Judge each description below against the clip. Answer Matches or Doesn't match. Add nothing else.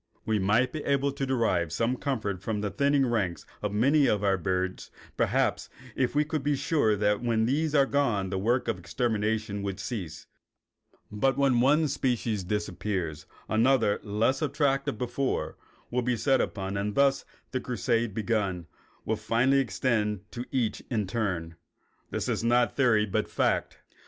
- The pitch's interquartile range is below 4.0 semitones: Doesn't match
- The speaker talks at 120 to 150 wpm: Doesn't match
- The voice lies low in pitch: Matches